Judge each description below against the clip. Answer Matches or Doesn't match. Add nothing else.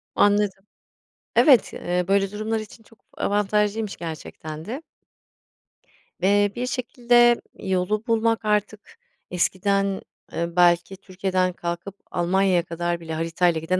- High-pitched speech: Matches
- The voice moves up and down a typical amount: Matches